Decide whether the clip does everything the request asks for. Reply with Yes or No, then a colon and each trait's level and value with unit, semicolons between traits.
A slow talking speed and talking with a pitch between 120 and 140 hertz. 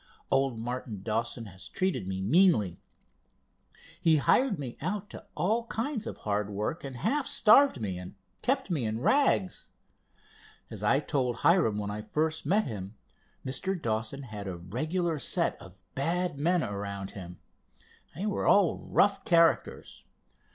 No: average, 150 wpm; low, 135 Hz